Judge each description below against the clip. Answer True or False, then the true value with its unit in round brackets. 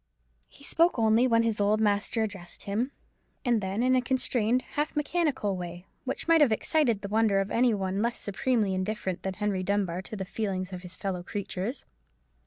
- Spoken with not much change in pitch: False (4.2 semitones)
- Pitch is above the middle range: True (210 Hz)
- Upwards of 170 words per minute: True (190 wpm)